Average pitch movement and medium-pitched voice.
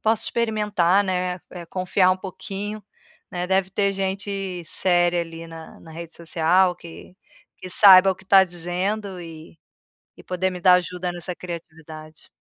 No: narrow, 2.1 semitones; medium, 180 Hz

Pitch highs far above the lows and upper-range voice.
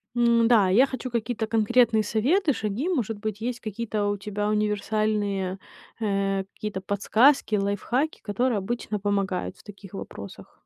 No: average, 2.8 semitones; high, 215 Hz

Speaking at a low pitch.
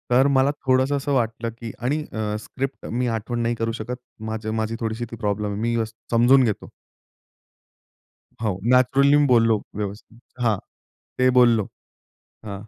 Yes: low, 115 Hz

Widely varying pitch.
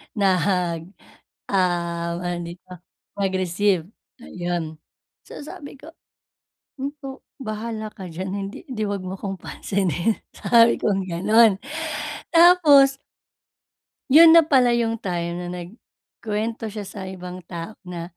No: average, 4.7 semitones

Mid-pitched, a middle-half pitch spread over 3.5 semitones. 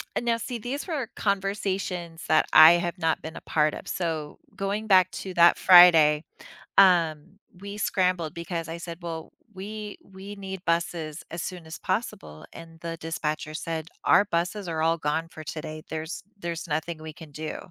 No: medium, 170 Hz; average, 3.2 semitones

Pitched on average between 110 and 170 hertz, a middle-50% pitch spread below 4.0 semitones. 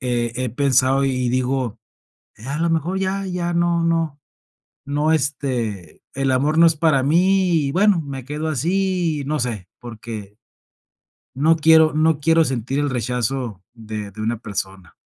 No: medium, 140 Hz; average, 5.2 semitones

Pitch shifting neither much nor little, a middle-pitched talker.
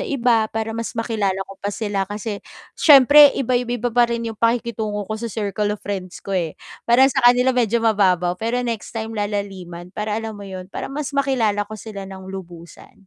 No: average, 3.1 semitones; high, 220 Hz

